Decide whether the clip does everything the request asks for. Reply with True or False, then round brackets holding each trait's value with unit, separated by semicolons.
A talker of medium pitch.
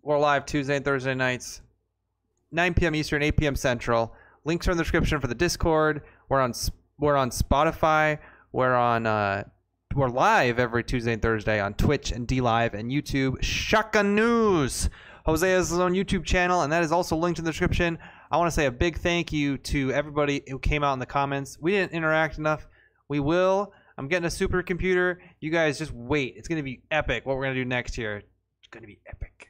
True (145 Hz)